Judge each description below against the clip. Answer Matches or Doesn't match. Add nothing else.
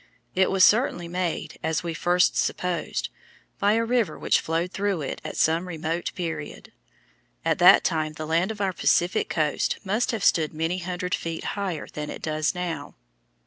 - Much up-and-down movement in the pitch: Doesn't match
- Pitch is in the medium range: Matches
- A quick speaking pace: Doesn't match